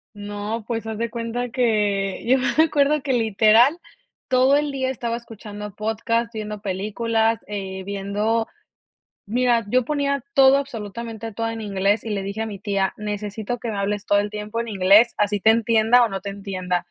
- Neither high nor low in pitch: No, high, 220 Hz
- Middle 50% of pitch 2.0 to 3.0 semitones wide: Yes, narrow, 2.5 semitones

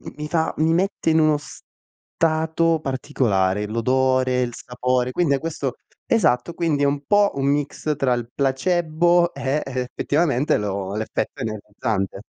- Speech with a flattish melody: No, average, 4.4 semitones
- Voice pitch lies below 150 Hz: Yes, medium, 140 Hz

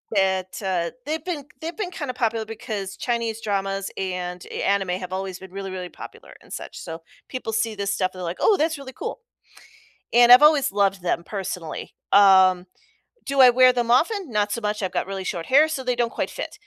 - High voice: Yes, high, 205 Hz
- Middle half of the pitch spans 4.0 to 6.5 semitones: Yes, average, 5.1 semitones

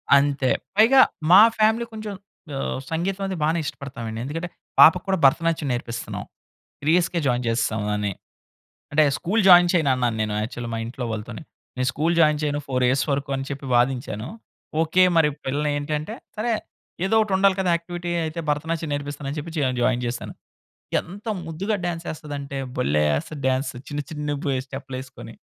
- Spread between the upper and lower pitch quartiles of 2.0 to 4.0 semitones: No, average, 5.0 semitones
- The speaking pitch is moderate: Yes, medium, 150 Hz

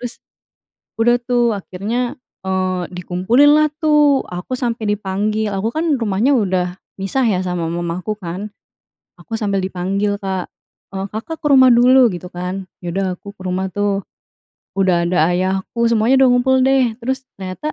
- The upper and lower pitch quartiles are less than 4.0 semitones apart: No, average, 4.8 semitones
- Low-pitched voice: No, high, 205 Hz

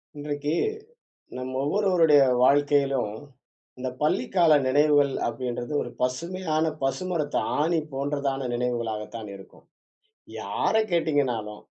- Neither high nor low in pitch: Yes, medium, 145 Hz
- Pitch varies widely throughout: No, average, 3.6 semitones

